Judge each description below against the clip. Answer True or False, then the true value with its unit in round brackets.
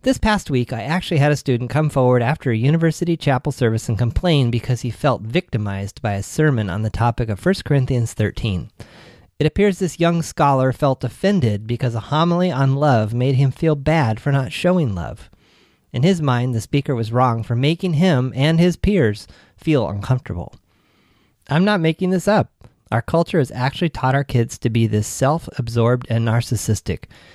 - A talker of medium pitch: False (130 Hz)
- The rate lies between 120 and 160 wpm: False (185 wpm)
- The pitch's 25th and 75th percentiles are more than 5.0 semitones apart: True (5.4 semitones)